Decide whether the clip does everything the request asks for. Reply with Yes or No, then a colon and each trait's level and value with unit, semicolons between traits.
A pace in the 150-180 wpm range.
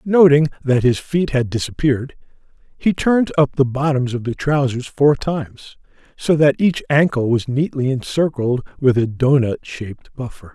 Yes: average, 160 wpm